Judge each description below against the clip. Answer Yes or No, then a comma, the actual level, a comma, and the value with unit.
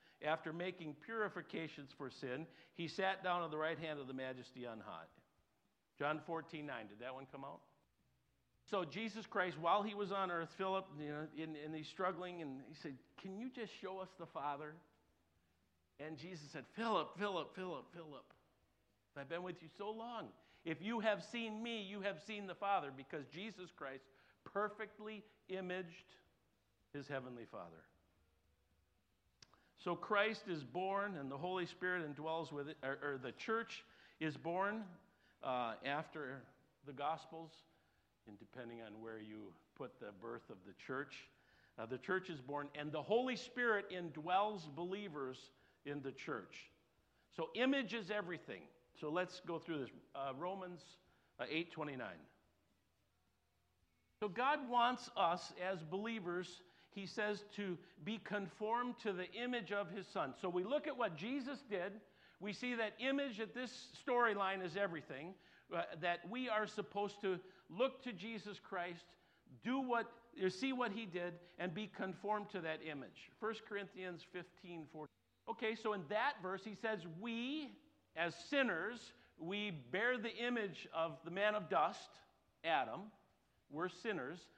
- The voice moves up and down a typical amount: No, wide, 5.8 semitones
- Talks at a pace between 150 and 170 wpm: Yes, average, 155 wpm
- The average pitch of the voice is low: No, medium, 180 Hz